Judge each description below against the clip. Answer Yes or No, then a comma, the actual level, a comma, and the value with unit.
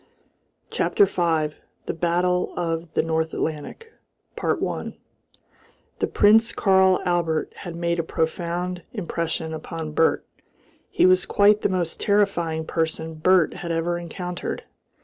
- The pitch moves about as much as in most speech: No, narrow, 2.1 semitones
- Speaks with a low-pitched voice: No, medium, 170 Hz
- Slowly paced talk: Yes, slow, 125 wpm